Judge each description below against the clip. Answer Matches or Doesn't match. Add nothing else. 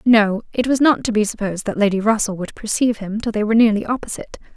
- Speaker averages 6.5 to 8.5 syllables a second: Matches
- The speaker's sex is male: Doesn't match